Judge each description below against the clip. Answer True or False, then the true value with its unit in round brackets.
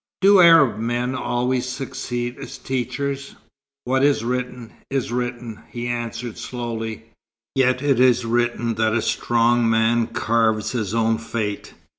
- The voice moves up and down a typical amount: False (1.9 semitones)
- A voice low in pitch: True (120 Hz)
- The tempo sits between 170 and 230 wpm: False (135 wpm)